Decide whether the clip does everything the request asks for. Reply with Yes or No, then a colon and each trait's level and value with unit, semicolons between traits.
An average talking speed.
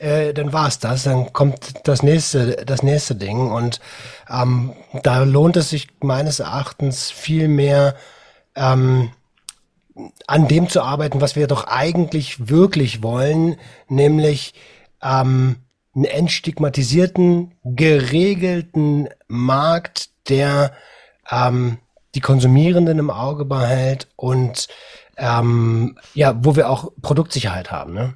No: slow, 115 wpm